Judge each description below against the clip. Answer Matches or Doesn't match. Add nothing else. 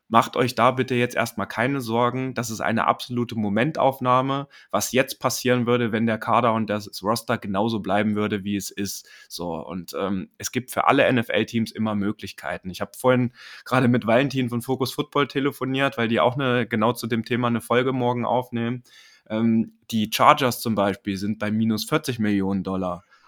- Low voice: Matches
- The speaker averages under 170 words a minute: Doesn't match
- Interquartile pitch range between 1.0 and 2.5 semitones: Doesn't match